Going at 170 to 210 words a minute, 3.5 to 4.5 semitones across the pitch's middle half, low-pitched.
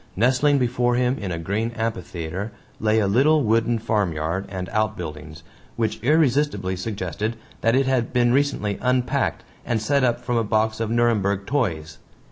No: average, 160 wpm; average, 3.9 semitones; low, 110 Hz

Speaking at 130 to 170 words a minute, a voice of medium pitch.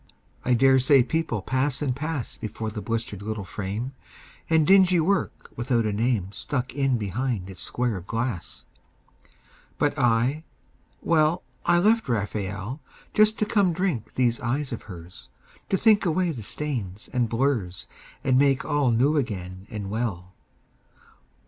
No: average, 150 wpm; low, 125 Hz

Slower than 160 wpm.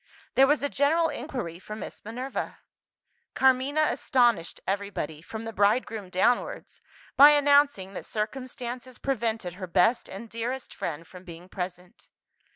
Yes: average, 140 wpm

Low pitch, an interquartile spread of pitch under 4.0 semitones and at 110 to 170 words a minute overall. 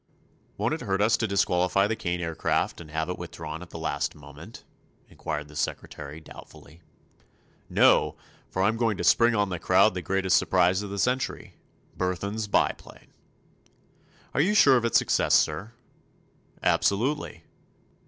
No: very low, 95 Hz; average, 4.6 semitones; average, 150 wpm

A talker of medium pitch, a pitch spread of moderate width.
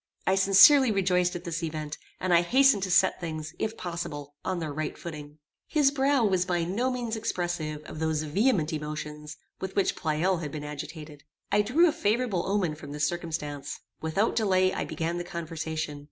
Yes: medium, 175 Hz; average, 4.4 semitones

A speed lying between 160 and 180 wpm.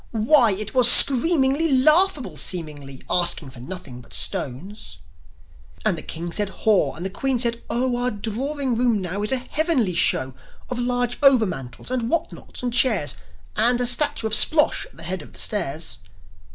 Yes: average, 170 wpm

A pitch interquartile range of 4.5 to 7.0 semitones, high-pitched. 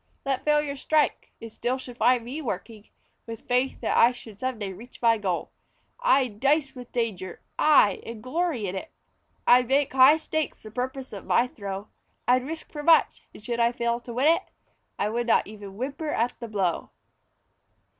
No: average, 4.0 semitones; high, 245 Hz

